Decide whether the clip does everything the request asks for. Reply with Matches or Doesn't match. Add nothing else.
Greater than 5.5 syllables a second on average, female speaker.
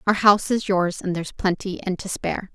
Matches